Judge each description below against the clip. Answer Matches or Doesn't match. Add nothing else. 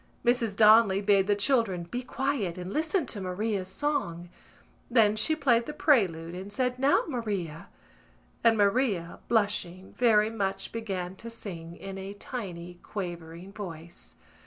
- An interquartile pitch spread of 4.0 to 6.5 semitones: Matches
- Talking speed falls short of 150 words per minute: Matches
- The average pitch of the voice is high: Matches